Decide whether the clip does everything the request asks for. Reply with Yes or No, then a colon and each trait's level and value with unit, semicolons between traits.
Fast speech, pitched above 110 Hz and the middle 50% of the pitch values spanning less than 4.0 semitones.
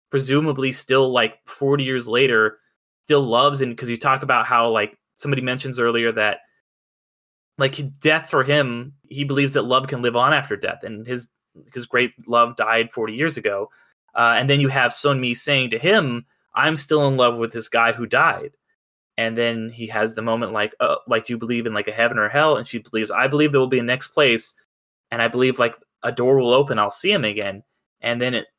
Yes: fast, 220 wpm; low, 125 Hz; average, 3.1 semitones